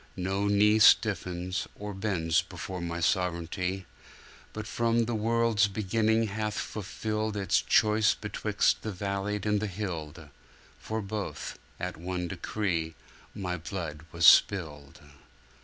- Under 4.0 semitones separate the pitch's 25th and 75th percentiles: Yes, average, 3.2 semitones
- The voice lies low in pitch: Yes, low, 100 Hz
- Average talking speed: No, slow, 125 wpm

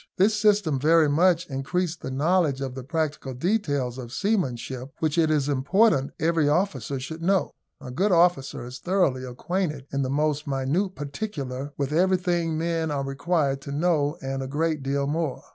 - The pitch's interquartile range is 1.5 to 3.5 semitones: No, average, 4.3 semitones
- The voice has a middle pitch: Yes, medium, 150 Hz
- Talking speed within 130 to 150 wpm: No, average, 170 wpm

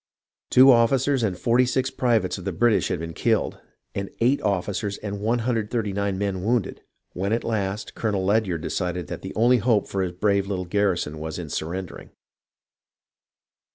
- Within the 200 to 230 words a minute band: No, average, 155 wpm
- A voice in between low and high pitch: No, low, 100 Hz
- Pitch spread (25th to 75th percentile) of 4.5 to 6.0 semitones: No, average, 3.9 semitones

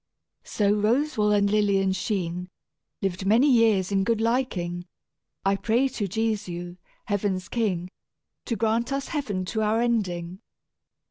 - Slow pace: Yes, slow, 130 wpm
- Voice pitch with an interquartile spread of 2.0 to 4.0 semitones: Yes, average, 3.6 semitones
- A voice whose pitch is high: Yes, high, 205 Hz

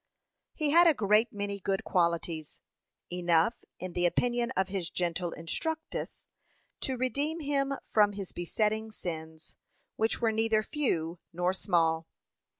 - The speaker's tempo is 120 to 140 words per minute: Yes, slow, 135 wpm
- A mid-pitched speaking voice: No, high, 200 Hz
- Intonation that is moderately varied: No, wide, 5.7 semitones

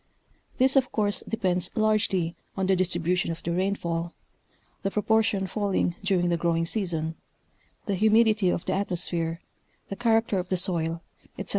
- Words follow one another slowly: No, average, 150 wpm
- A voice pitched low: No, medium, 185 Hz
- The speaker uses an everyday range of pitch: Yes, average, 3.7 semitones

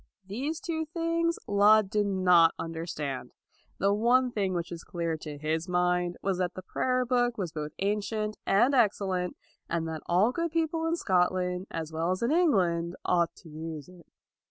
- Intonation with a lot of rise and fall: Yes, wide, 5.9 semitones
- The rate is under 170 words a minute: No, average, 180 wpm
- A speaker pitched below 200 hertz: Yes, medium, 185 Hz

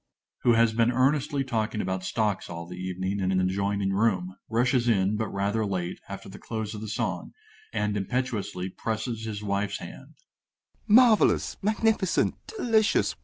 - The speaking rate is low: No, average, 160 wpm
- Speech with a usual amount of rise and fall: Yes, average, 3.9 semitones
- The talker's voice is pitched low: Yes, low, 105 Hz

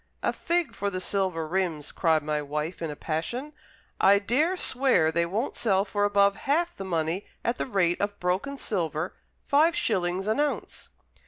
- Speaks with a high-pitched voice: Yes, high, 195 Hz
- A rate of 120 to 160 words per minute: No, average, 175 wpm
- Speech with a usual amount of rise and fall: No, wide, 6.2 semitones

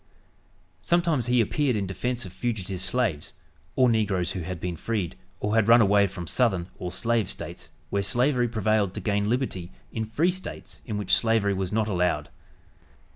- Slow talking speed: No, average, 175 wpm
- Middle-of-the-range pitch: No, low, 105 Hz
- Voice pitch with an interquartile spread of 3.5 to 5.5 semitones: Yes, average, 4.2 semitones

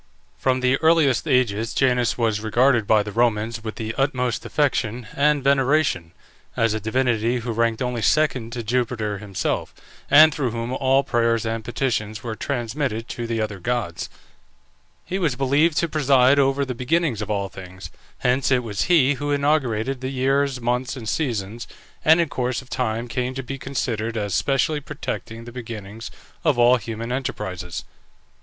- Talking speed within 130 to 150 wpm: No, average, 165 wpm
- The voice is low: Yes, low, 125 Hz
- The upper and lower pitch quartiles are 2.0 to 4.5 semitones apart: Yes, average, 3.4 semitones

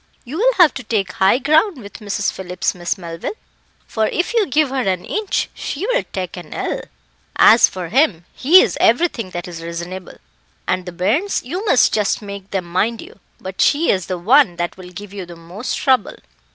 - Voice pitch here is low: No, high, 205 Hz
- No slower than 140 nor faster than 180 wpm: No, average, 195 wpm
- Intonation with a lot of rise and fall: Yes, wide, 7.6 semitones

